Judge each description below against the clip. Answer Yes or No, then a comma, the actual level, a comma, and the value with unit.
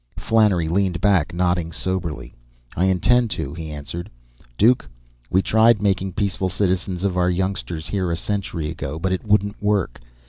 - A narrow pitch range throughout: No, average, 3.2 semitones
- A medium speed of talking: Yes, average, 160 wpm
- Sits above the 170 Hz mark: No, very low, 95 Hz